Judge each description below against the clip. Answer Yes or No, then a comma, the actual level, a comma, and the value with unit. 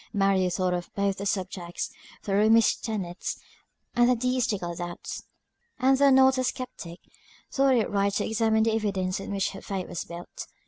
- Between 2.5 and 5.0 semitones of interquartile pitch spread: Yes, average, 3.8 semitones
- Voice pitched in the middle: No, high, 200 Hz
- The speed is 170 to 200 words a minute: Yes, average, 175 wpm